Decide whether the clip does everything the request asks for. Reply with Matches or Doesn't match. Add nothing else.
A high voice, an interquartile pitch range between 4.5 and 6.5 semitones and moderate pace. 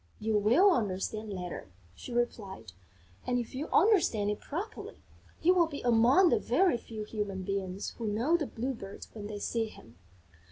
Matches